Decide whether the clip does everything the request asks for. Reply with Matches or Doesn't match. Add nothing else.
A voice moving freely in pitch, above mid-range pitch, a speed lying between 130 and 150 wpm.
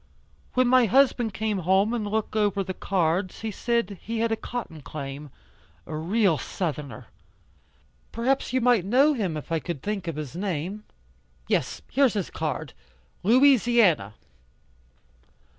Matches